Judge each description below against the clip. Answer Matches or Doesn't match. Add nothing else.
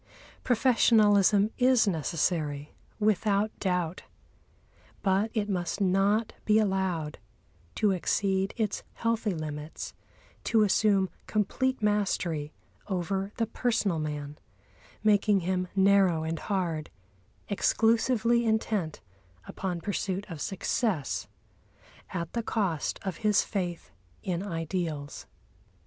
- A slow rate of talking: Matches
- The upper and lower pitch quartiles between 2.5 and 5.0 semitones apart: Matches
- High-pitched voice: Matches